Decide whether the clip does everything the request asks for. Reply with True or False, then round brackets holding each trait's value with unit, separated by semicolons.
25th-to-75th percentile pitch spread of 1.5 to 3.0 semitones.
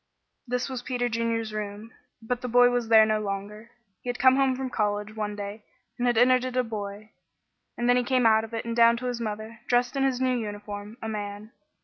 True (2.6 semitones)